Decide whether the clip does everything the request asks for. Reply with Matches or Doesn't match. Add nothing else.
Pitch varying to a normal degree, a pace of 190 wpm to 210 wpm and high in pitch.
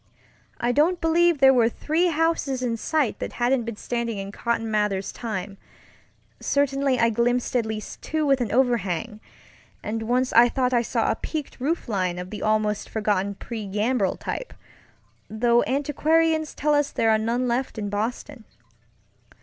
Doesn't match